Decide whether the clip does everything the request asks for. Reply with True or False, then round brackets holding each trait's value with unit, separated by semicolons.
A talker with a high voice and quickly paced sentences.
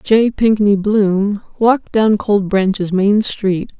False (205 Hz; 140 wpm)